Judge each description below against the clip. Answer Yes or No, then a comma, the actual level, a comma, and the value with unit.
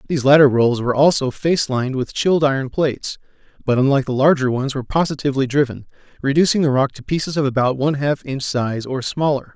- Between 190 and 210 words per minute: Yes, average, 200 wpm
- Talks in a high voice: No, low, 135 Hz